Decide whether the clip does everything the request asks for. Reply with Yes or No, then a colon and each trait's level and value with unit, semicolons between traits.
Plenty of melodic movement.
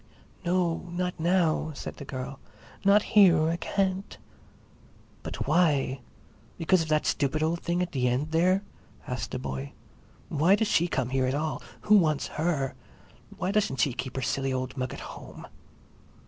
No: average, 5.0 semitones